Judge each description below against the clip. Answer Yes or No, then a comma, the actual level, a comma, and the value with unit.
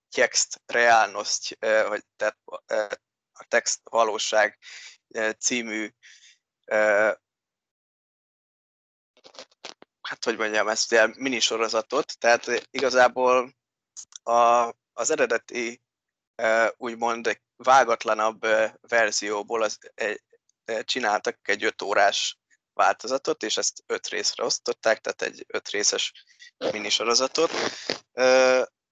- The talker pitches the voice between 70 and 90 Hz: No, low, 120 Hz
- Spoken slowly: Yes, slow, 85 wpm